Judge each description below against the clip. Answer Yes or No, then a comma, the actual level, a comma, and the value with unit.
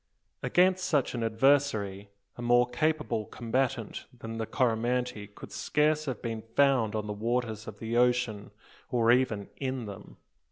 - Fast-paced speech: No, average, 150 wpm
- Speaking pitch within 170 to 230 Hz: No, low, 120 Hz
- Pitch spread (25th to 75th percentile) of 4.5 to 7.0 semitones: No, average, 3.0 semitones